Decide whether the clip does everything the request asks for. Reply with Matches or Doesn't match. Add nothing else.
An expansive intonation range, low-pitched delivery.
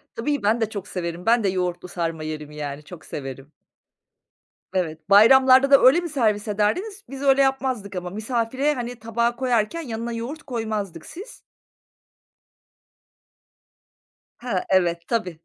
Doesn't match